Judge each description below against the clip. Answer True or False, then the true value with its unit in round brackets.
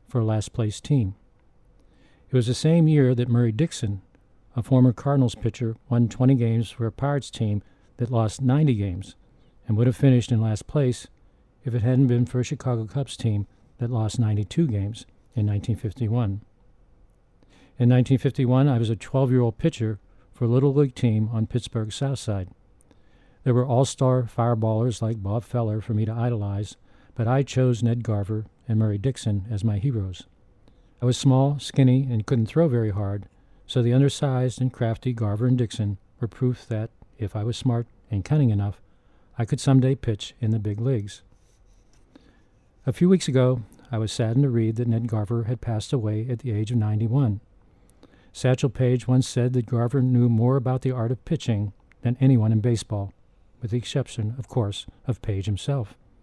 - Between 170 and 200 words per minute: True (180 wpm)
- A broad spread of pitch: False (3.3 semitones)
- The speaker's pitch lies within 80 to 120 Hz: True (115 Hz)